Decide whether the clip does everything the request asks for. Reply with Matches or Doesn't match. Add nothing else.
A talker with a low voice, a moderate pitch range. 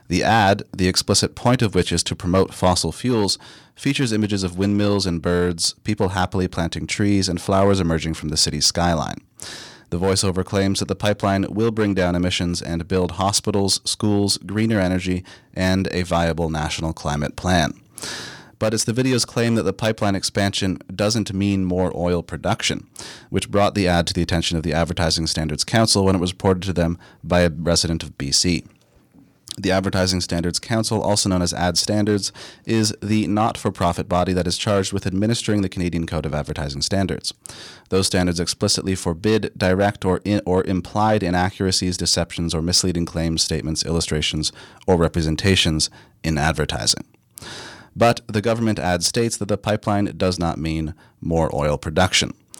Matches